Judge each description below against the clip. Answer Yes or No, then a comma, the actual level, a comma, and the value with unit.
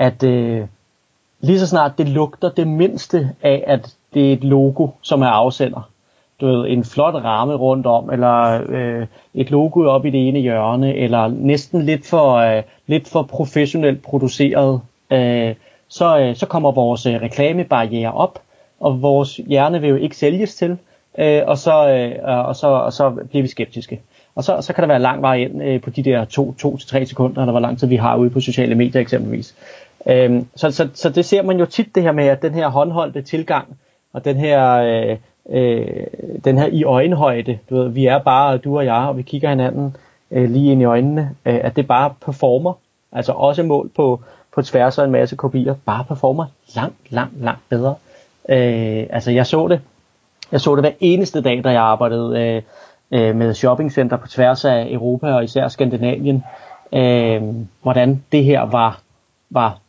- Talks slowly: No, average, 190 wpm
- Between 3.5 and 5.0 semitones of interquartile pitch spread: No, average, 3.1 semitones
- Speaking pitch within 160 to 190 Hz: No, low, 130 Hz